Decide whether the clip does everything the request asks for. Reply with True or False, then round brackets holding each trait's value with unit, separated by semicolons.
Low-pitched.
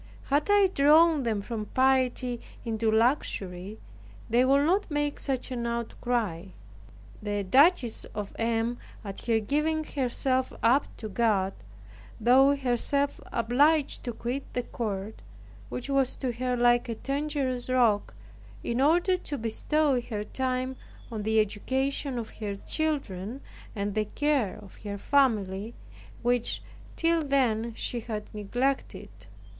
False (245 Hz)